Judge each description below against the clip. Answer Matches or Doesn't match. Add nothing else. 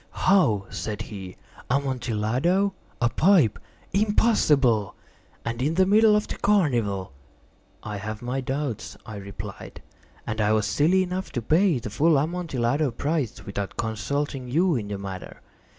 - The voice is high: Doesn't match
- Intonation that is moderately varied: Doesn't match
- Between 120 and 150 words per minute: Matches